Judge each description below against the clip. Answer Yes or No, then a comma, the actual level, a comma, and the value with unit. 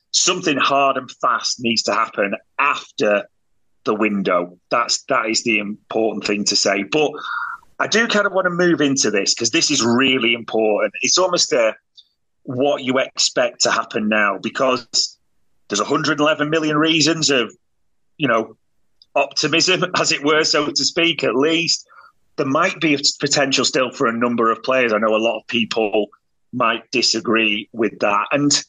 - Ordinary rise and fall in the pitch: No, wide, 6.1 semitones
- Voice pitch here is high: No, medium, 140 Hz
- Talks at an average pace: Yes, average, 170 wpm